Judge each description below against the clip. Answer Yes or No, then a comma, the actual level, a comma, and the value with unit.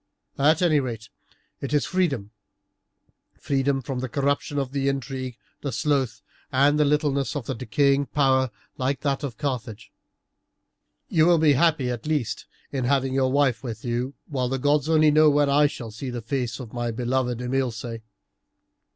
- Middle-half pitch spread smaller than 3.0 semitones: Yes, narrow, 2.6 semitones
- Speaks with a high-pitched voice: No, low, 135 Hz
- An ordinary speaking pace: Yes, average, 165 wpm